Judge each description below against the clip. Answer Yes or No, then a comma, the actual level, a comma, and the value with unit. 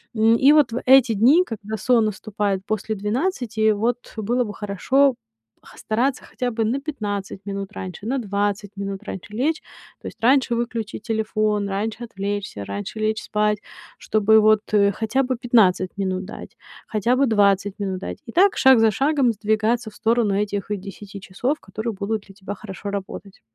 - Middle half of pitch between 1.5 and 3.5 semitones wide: Yes, average, 3.0 semitones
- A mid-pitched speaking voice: No, high, 215 Hz